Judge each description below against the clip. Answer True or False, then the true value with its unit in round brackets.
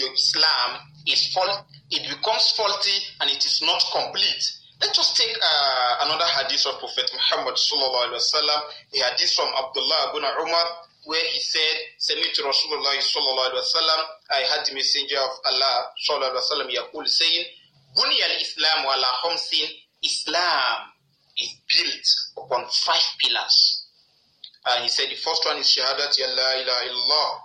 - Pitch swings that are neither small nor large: False (6.3 semitones)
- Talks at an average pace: True (150 wpm)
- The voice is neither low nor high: True (155 Hz)